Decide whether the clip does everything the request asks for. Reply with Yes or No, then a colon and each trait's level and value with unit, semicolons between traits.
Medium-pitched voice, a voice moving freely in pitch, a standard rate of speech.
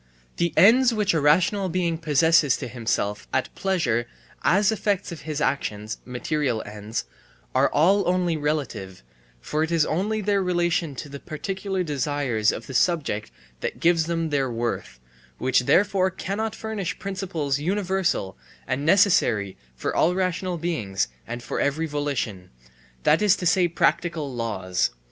Yes: medium, 160 Hz; wide, 6.3 semitones; average, 150 wpm